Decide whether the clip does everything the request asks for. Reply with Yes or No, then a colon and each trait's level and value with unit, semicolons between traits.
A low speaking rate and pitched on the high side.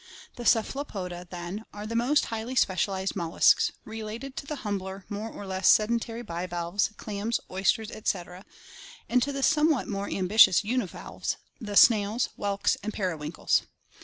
No: average, 145 wpm; high, 210 Hz